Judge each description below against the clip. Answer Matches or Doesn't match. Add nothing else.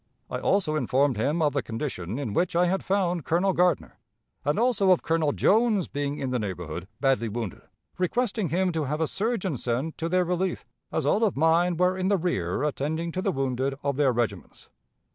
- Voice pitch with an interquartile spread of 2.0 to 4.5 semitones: Doesn't match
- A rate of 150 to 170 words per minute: Doesn't match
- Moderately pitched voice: Matches